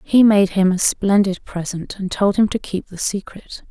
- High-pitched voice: Yes, high, 195 Hz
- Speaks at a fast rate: Yes, fast, 210 wpm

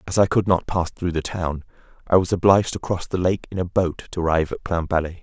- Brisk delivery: Yes, fast, 255 wpm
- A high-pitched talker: No, very low, 90 Hz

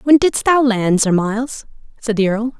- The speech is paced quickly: Yes, fast, 210 wpm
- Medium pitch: No, high, 230 Hz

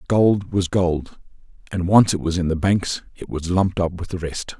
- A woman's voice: No, male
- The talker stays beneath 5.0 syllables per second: Yes, 4.7 syllables/s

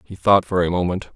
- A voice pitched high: No, very low, 95 Hz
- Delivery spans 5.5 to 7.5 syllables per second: Yes, 5.8 syllables/s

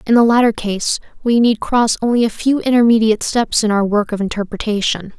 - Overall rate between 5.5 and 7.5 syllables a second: Yes, 5.7 syllables/s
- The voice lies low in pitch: No, high, 220 Hz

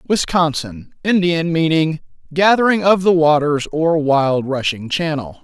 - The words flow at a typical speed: No, slow, 110 wpm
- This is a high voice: No, medium, 160 Hz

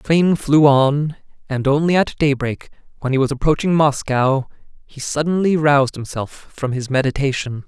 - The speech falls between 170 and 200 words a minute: No, average, 155 wpm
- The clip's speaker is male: Yes, male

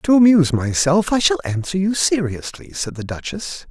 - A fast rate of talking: No, average, 180 wpm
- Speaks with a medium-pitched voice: Yes, medium, 160 Hz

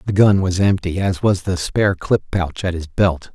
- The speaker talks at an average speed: No, fast, 235 wpm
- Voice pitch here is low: Yes, very low, 90 Hz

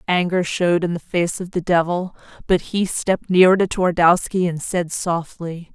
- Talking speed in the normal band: Yes, average, 180 wpm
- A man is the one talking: No, female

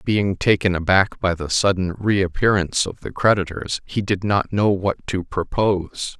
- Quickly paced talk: No, average, 165 wpm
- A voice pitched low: Yes, very low, 95 Hz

